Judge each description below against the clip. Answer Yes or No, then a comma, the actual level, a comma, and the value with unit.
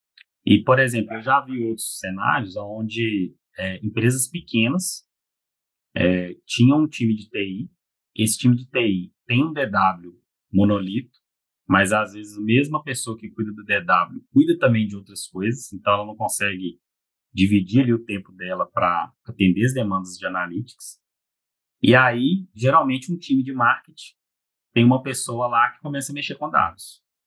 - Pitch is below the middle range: Yes, low, 115 Hz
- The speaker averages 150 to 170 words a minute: Yes, average, 160 wpm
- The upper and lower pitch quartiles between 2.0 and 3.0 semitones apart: No, average, 4.8 semitones